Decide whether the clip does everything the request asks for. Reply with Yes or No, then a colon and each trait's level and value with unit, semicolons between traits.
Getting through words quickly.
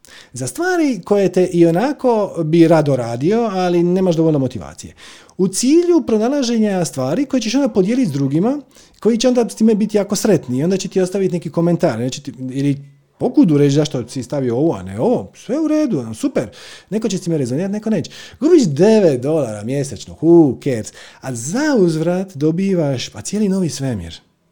Yes: fast, 180 wpm